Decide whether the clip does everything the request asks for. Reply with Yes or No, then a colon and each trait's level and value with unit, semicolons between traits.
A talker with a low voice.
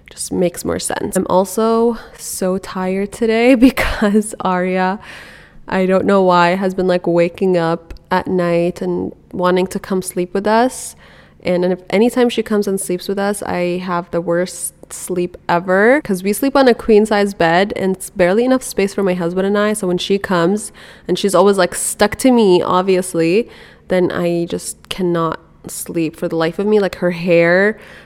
No: medium, 185 Hz